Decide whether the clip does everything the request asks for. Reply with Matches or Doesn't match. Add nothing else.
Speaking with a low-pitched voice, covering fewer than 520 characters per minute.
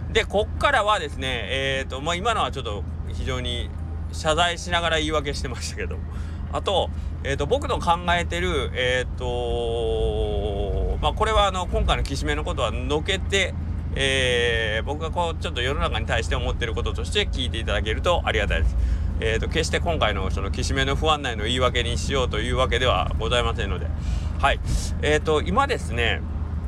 Matches